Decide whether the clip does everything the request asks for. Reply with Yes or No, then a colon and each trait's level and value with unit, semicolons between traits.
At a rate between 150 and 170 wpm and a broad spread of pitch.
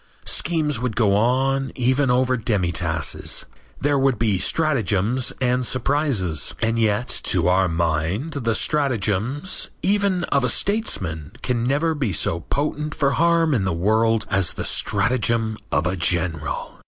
No: average, 140 wpm; wide, 6.5 semitones